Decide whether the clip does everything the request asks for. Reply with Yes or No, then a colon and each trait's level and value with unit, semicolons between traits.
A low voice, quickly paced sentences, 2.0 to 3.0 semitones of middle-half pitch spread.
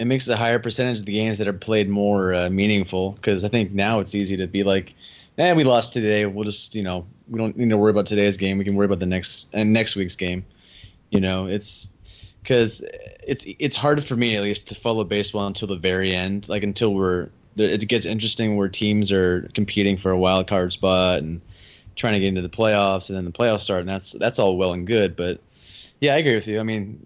Yes: low, 100 Hz; fast, 245 wpm; narrow, 2.5 semitones